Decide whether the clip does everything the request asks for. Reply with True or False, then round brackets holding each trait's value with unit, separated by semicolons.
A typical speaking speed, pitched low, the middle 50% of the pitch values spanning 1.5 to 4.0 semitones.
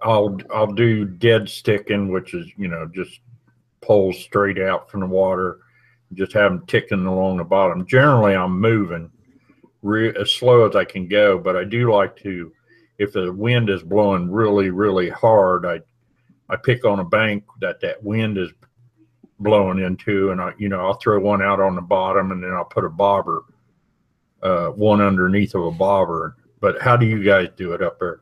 True (195 wpm; 100 Hz; 2.7 semitones)